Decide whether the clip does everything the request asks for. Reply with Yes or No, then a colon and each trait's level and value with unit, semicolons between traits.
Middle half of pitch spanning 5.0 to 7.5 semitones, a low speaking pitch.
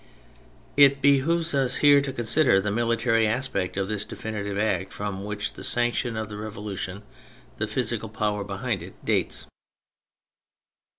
No: average, 4.1 semitones; low, 110 Hz